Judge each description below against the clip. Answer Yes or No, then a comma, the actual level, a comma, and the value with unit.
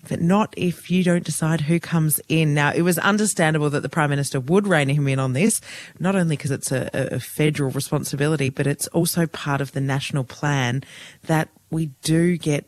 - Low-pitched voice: No, medium, 155 Hz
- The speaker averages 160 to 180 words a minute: No, fast, 205 wpm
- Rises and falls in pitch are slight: No, average, 3.2 semitones